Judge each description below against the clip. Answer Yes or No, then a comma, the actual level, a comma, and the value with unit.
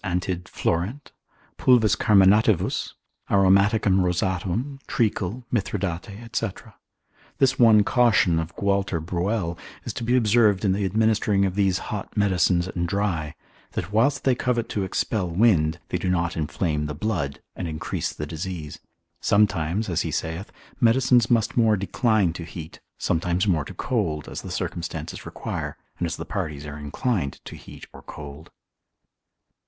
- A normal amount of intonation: Yes, average, 4.5 semitones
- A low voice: Yes, very low, 95 Hz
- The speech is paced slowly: No, average, 150 wpm